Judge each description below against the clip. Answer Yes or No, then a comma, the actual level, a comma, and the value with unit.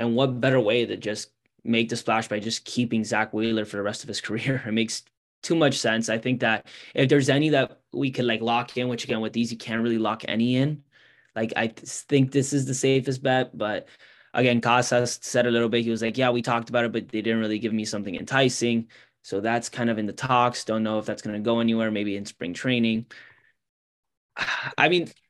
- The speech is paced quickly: Yes, fast, 235 wpm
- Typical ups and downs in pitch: No, narrow, 2.1 semitones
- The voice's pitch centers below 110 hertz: No, low, 115 Hz